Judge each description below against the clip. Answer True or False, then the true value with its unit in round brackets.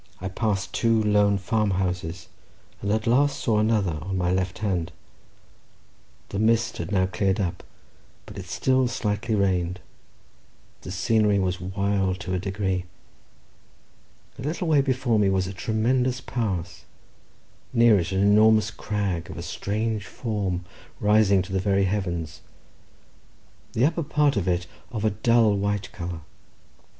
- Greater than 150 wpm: False (140 wpm)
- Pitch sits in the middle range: False (100 Hz)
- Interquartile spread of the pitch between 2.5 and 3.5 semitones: True (3.1 semitones)